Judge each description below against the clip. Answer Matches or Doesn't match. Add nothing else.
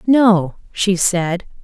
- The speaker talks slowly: Matches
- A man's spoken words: Doesn't match